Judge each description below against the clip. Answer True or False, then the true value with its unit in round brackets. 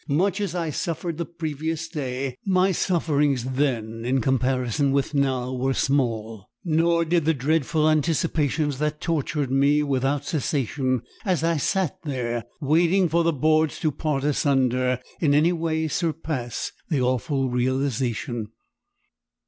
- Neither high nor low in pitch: True (145 Hz)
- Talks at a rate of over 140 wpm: False (135 wpm)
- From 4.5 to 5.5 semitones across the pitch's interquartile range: False (3.9 semitones)